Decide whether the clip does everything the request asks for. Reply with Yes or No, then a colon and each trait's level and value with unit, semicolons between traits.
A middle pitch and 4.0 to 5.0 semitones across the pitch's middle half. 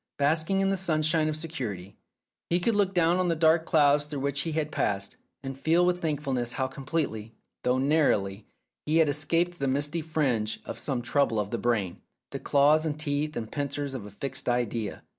Yes: medium, 145 Hz; average, 4.6 semitones